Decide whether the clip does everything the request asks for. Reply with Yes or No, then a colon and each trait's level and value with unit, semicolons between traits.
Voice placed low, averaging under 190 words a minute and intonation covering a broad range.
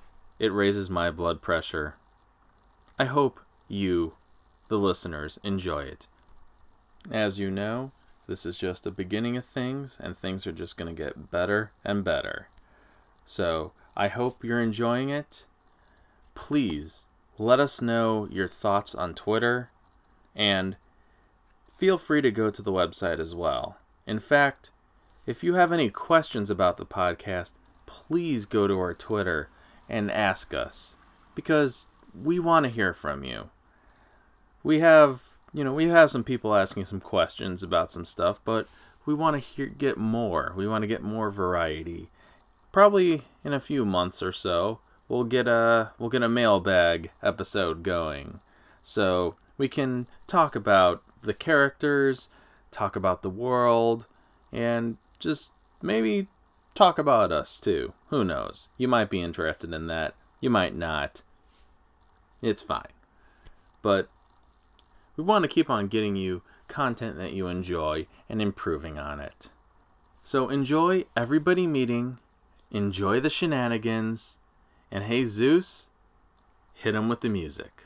Yes: low, 105 Hz; average, 140 wpm; wide, 6.0 semitones